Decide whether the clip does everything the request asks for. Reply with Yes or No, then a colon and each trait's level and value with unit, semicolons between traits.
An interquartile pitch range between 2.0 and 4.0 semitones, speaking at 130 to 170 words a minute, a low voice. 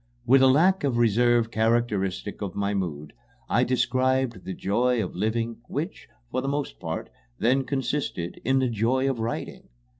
Yes: average, 3.5 semitones; average, 160 wpm; low, 120 Hz